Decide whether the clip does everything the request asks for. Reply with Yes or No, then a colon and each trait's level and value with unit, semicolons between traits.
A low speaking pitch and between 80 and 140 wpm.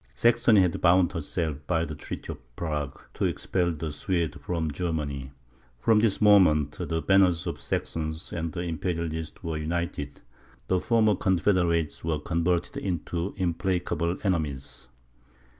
Yes: very low, 85 Hz; slow, 135 wpm